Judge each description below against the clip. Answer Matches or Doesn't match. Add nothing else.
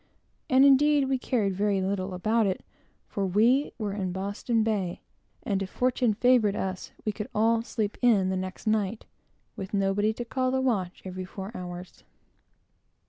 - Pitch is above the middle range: Matches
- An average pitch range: Matches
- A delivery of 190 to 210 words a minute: Doesn't match